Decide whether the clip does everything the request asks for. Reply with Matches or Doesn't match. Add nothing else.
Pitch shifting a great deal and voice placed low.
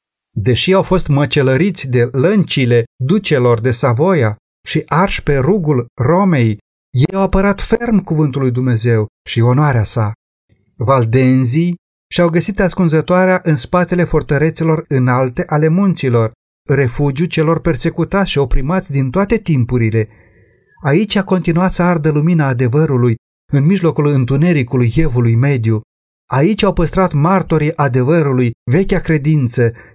Doesn't match